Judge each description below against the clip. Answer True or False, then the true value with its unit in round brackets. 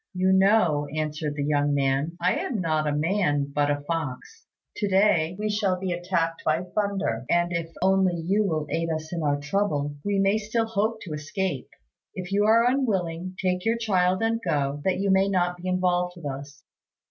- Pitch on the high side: False (180 Hz)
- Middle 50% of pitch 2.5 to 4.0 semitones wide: False (4.5 semitones)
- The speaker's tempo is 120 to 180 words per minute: False (195 wpm)